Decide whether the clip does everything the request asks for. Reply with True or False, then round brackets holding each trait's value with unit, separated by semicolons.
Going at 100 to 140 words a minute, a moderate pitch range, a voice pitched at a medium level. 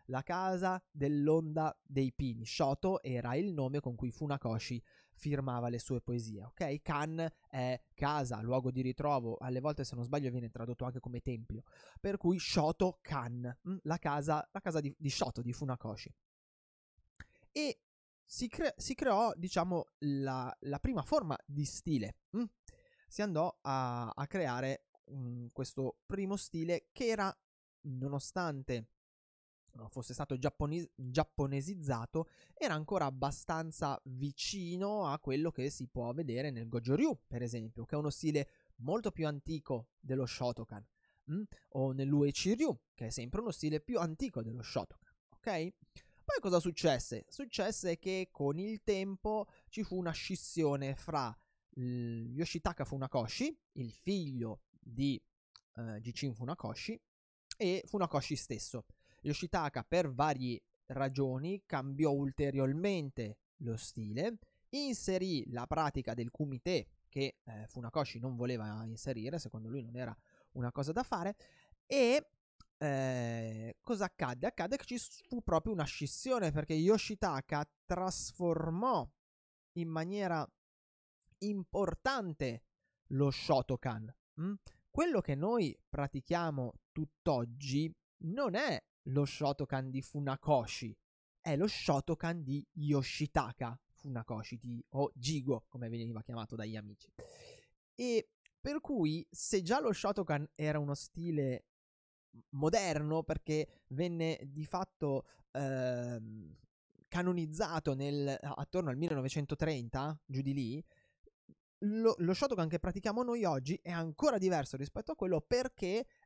False (125 wpm; 5.7 semitones; 145 Hz)